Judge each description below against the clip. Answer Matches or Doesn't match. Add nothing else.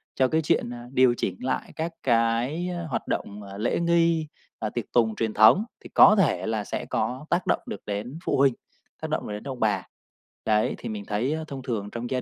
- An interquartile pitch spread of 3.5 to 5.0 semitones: Doesn't match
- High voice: Doesn't match